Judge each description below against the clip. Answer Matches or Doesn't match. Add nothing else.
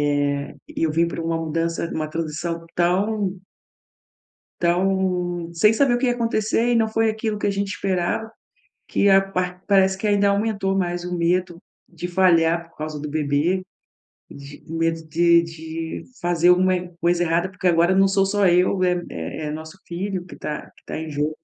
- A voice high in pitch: Doesn't match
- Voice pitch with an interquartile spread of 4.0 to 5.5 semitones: Doesn't match